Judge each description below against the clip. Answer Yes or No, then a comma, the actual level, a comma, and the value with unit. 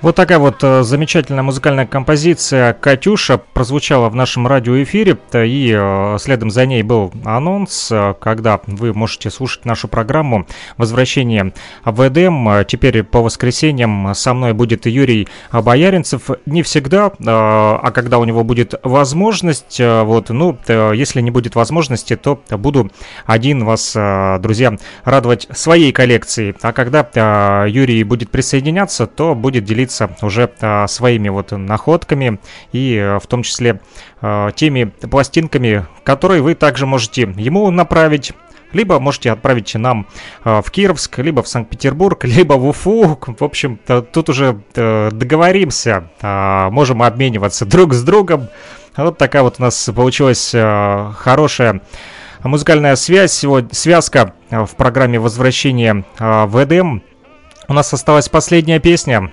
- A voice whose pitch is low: Yes, low, 125 Hz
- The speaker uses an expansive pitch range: No, average, 4.5 semitones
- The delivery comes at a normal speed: Yes, average, 130 wpm